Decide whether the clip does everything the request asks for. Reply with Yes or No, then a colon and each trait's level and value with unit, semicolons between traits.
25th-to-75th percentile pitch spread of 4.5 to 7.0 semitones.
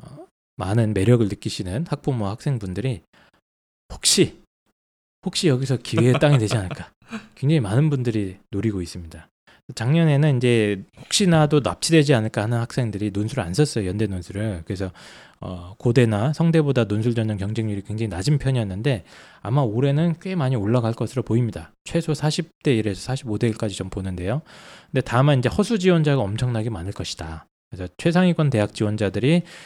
Yes: wide, 6.2 semitones